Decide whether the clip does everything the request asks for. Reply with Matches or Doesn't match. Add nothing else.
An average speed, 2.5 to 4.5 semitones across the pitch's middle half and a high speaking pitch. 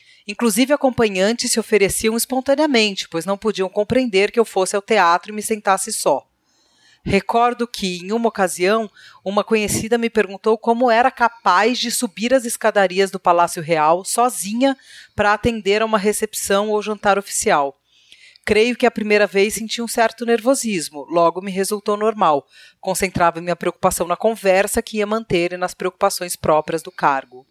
Matches